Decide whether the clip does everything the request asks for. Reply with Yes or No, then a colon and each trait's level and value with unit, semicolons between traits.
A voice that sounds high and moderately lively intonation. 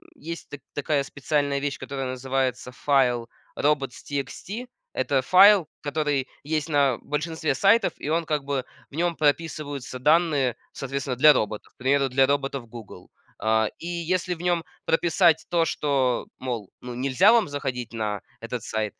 No: medium, 140 Hz; average, 3.8 semitones